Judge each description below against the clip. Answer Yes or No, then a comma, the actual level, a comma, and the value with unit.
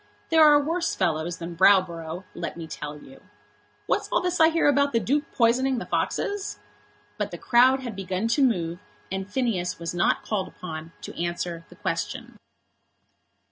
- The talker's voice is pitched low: No, high, 200 Hz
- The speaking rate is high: No, average, 170 wpm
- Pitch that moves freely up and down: Yes, wide, 8.0 semitones